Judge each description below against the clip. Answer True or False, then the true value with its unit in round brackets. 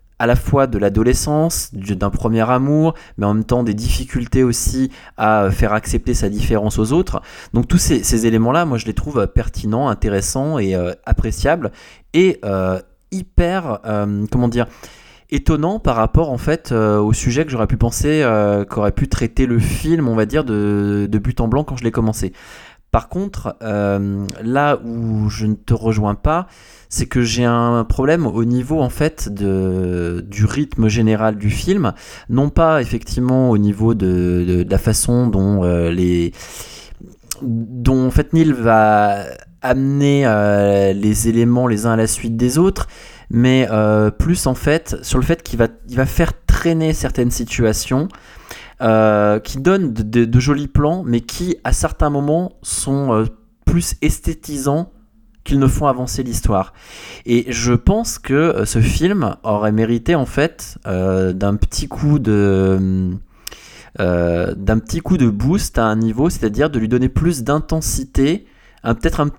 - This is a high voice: False (115 Hz)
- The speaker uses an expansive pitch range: False (4.6 semitones)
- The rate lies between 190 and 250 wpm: False (170 wpm)